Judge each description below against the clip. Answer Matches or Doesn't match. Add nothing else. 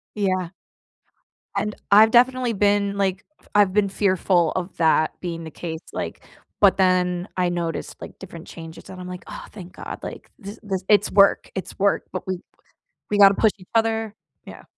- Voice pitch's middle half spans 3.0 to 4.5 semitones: Doesn't match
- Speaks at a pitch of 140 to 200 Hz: Matches